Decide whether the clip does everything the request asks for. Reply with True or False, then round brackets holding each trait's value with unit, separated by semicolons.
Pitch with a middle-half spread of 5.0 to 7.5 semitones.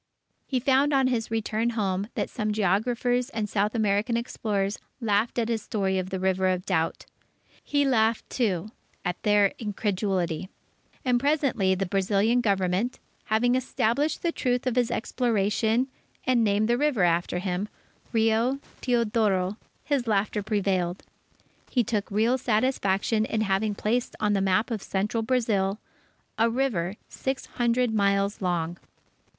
False (3.7 semitones)